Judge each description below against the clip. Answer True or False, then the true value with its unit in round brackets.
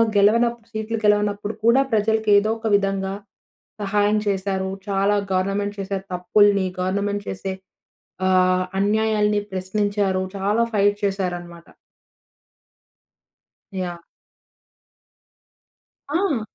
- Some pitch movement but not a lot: False (1.8 semitones)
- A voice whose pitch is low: False (205 Hz)